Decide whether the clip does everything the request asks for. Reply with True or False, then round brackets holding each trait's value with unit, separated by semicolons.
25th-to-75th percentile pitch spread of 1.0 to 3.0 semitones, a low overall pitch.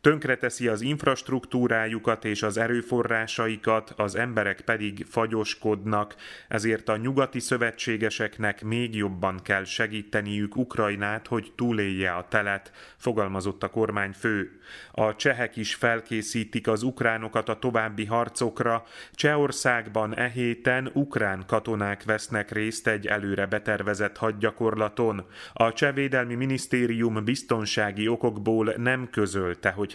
True (2.4 semitones; 110 Hz)